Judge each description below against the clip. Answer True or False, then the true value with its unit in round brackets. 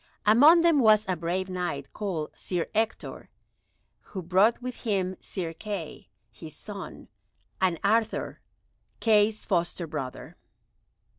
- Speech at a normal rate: False (120 wpm)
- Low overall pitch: False (190 Hz)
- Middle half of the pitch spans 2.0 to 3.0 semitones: False (4.2 semitones)